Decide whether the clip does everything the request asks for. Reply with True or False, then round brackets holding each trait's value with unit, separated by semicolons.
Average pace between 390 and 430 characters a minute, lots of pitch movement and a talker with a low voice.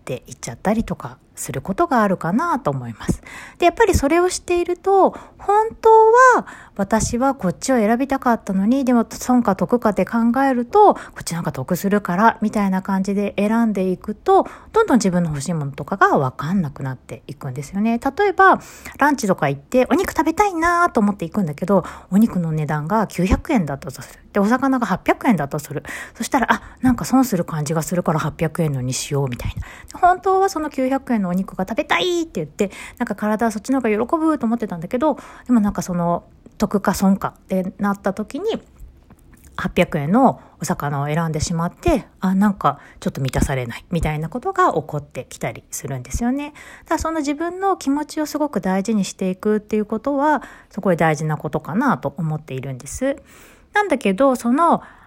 False (400 characters per minute; 8.2 semitones; 205 Hz)